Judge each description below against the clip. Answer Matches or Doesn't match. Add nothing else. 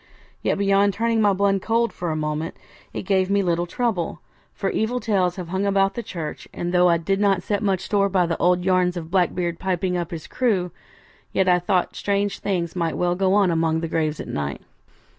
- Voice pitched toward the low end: Doesn't match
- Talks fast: Matches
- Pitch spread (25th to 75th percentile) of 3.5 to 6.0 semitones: Doesn't match